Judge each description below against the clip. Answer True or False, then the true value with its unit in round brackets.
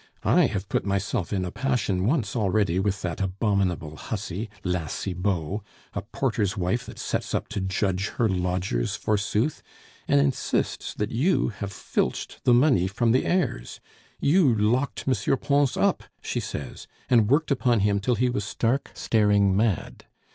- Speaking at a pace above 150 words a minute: True (160 wpm)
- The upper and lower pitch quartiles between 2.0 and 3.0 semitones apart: False (4.4 semitones)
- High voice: False (105 Hz)